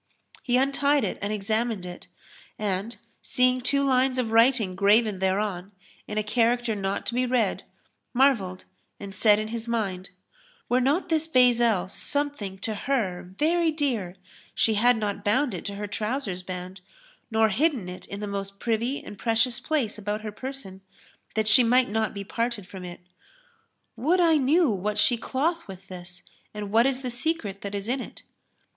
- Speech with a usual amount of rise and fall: Yes, average, 4.3 semitones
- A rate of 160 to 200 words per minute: Yes, average, 175 wpm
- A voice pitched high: Yes, high, 220 Hz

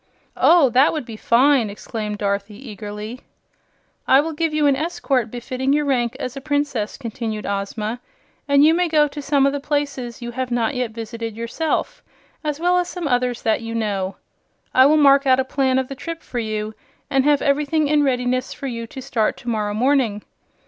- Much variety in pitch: No, average, 4.0 semitones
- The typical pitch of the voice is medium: No, very high, 260 Hz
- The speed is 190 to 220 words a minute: Yes, average, 195 wpm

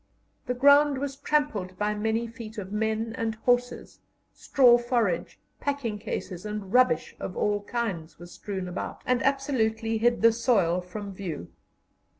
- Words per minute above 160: No, average, 150 wpm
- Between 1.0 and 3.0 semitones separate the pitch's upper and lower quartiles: No, average, 3.5 semitones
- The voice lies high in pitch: Yes, high, 225 Hz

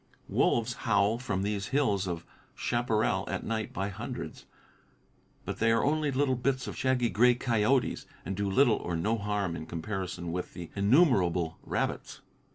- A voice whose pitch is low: Yes, low, 105 Hz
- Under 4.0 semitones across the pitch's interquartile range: No, average, 4.5 semitones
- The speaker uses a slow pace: No, average, 160 wpm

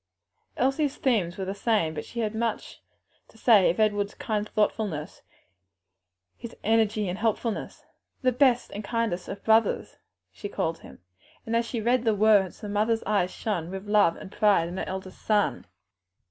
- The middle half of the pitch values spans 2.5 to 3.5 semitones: Yes, average, 2.9 semitones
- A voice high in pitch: Yes, high, 210 Hz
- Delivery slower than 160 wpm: No, average, 170 wpm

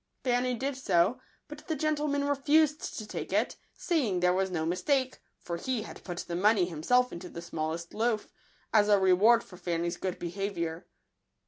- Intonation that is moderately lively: No, wide, 6.8 semitones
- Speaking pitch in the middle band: No, high, 205 Hz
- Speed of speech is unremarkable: Yes, average, 180 wpm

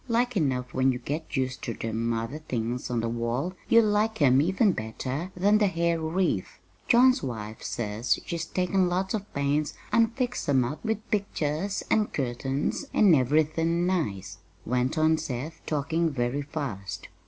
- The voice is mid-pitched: Yes, medium, 155 Hz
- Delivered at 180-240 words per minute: No, average, 165 wpm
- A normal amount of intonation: No, wide, 7.0 semitones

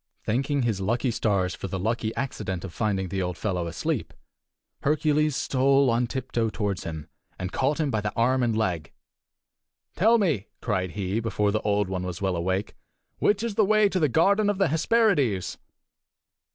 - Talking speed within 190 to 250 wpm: No, average, 175 wpm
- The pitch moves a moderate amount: No, wide, 7.5 semitones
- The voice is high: No, low, 115 Hz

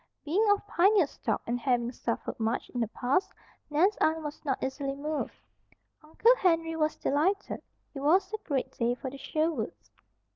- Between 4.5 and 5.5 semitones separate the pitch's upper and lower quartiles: Yes, average, 5.0 semitones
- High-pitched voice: Yes, very high, 300 Hz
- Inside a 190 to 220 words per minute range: No, average, 170 wpm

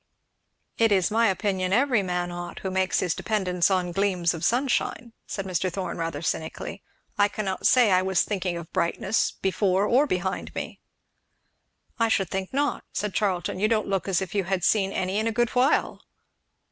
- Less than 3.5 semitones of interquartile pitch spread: Yes, average, 2.8 semitones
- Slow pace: No, average, 185 wpm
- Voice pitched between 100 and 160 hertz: No, high, 190 Hz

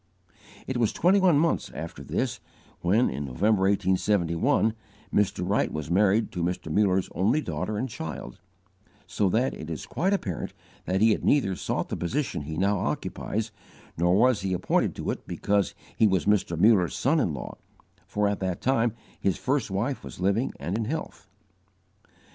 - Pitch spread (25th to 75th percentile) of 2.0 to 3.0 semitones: No, average, 4.3 semitones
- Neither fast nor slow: Yes, average, 170 wpm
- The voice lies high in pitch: No, low, 100 Hz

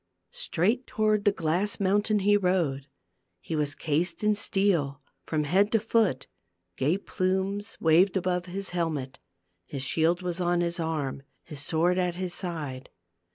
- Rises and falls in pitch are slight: No, average, 3.9 semitones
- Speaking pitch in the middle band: Yes, medium, 180 Hz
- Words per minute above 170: No, average, 150 wpm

